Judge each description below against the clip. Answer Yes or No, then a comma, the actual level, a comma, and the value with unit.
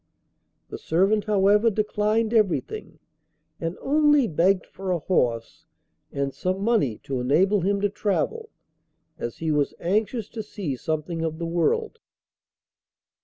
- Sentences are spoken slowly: Yes, slow, 130 wpm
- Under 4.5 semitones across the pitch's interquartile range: No, average, 4.9 semitones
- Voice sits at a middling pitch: No, high, 195 Hz